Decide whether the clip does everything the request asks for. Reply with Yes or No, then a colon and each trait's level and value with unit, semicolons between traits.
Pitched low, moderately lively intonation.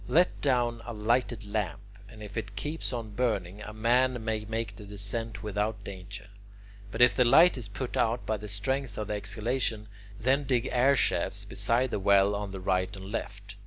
Yes: low, 110 Hz; average, 3.2 semitones